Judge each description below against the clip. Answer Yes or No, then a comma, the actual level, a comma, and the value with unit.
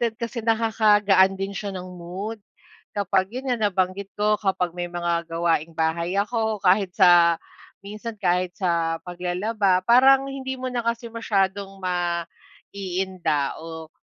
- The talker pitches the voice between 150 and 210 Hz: Yes, high, 190 Hz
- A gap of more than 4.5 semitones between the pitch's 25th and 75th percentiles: No, average, 3.9 semitones